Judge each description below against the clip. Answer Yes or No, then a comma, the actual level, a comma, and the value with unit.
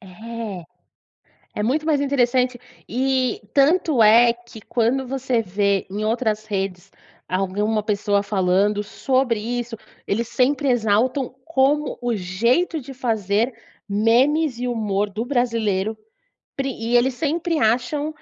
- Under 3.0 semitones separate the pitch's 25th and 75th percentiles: No, average, 4.1 semitones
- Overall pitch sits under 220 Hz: No, high, 235 Hz